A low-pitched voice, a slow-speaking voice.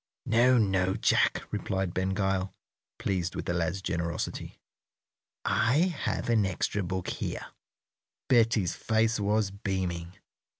Yes: very low, 95 Hz; slow, 120 wpm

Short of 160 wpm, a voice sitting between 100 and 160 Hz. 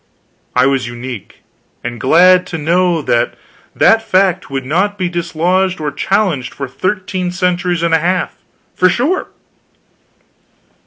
No: average, 140 wpm; medium, 175 Hz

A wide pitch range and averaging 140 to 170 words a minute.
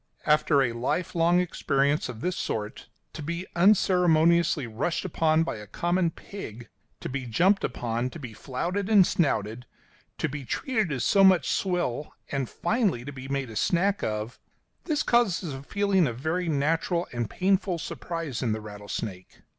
Yes: wide, 6.5 semitones; average, 165 wpm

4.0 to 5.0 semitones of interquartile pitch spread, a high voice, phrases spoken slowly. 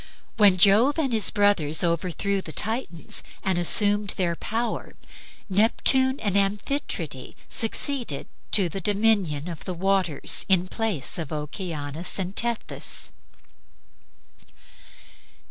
Yes: average, 4.3 semitones; high, 195 Hz; slow, 110 wpm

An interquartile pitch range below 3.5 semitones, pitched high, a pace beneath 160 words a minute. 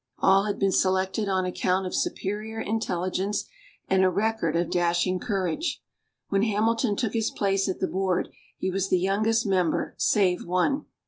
No: narrow, 2.6 semitones; high, 195 Hz; average, 165 wpm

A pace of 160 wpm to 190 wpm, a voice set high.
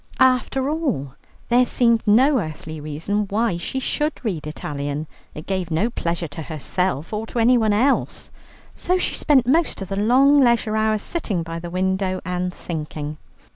Yes: average, 165 wpm; high, 205 Hz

